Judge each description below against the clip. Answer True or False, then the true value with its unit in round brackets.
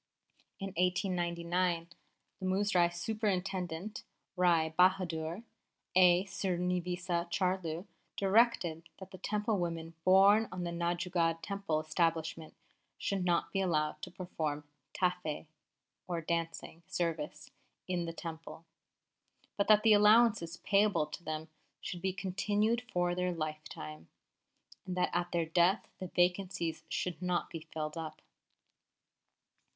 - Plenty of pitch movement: False (2.4 semitones)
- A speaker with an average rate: False (120 wpm)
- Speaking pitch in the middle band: True (175 Hz)